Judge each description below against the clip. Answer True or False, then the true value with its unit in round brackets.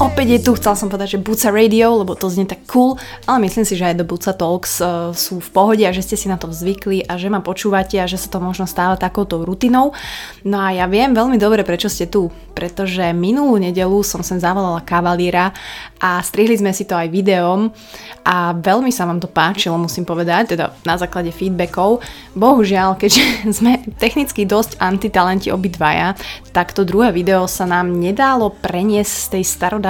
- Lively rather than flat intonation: False (2.9 semitones)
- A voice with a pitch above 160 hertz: True (190 Hz)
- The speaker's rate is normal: False (195 wpm)